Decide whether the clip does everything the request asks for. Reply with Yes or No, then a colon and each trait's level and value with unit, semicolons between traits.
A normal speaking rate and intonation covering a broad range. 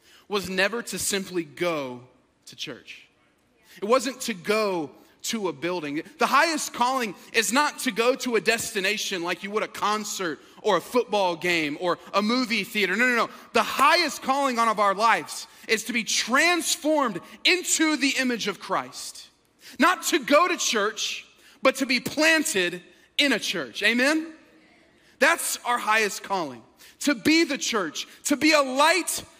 Yes: average, 165 wpm; wide, 6.3 semitones